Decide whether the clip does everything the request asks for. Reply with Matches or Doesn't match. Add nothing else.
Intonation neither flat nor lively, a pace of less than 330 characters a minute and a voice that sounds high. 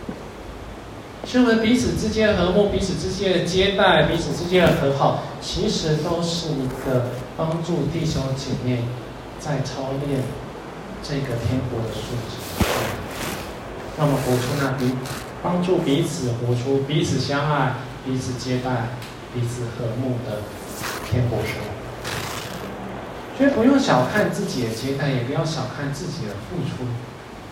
Doesn't match